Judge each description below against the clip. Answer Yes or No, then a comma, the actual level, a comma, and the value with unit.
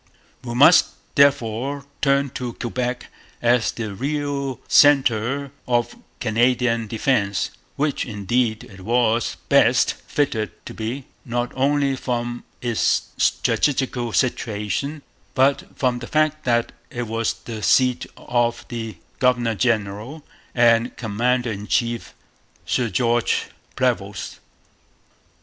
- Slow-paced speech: Yes, slow, 110 wpm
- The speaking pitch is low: Yes, low, 120 Hz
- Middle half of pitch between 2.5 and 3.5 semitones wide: Yes, average, 2.8 semitones